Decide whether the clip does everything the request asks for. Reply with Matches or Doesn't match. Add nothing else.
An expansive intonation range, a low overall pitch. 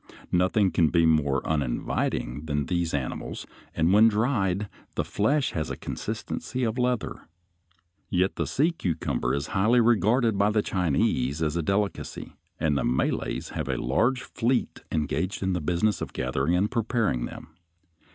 Matches